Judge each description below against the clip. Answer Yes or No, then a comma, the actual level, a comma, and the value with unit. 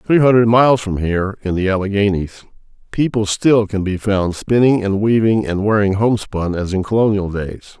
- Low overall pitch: Yes, low, 105 Hz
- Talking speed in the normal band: Yes, average, 175 wpm